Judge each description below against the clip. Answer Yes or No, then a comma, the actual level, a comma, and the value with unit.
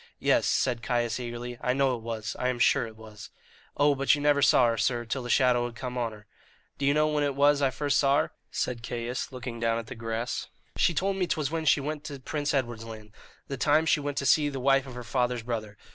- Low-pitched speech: Yes, low, 125 Hz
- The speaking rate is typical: No, fast, 250 wpm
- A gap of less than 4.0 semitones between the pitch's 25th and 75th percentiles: Yes, average, 3.4 semitones